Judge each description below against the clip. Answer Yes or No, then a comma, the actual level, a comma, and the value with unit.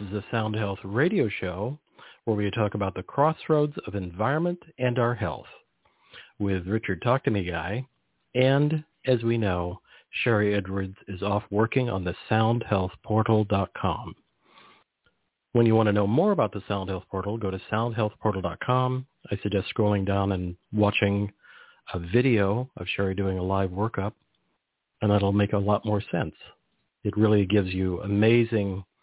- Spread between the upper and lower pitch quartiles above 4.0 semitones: No, average, 3.0 semitones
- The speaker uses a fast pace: No, average, 155 wpm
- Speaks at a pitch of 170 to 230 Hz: No, low, 105 Hz